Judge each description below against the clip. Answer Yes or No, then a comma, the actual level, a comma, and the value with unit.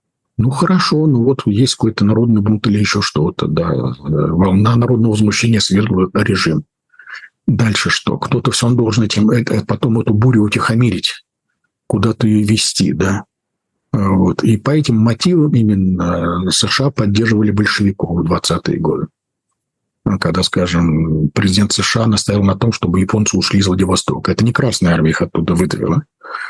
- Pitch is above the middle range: No, low, 110 Hz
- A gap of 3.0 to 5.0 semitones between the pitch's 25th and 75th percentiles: Yes, average, 3.6 semitones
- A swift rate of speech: No, average, 145 wpm